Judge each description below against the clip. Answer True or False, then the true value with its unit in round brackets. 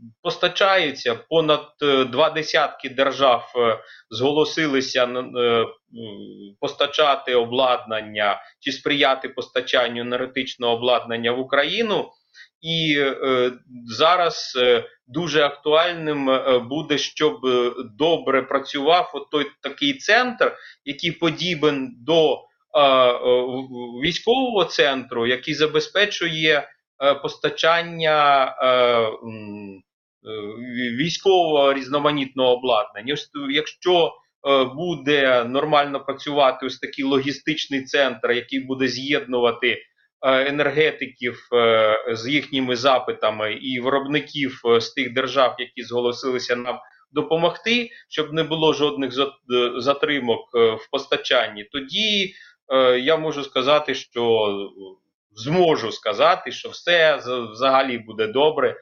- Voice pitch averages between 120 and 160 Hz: True (135 Hz)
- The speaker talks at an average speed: False (85 wpm)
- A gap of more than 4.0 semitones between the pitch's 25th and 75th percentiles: False (3.7 semitones)